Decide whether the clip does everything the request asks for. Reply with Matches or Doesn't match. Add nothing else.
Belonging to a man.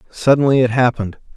Matches